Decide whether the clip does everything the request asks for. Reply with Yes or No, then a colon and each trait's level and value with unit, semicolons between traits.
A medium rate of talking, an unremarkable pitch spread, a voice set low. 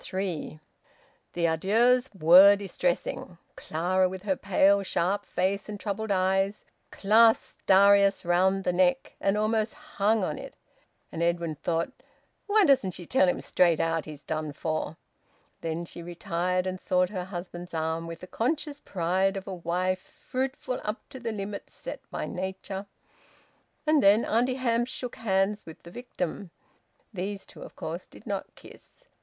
No: average, 155 wpm; average, 3.6 semitones; high, 190 Hz